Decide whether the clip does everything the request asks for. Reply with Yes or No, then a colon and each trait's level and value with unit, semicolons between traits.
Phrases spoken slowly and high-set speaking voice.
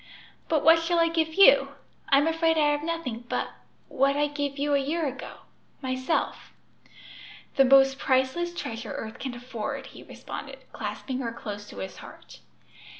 No: average, 160 wpm; very high, 280 Hz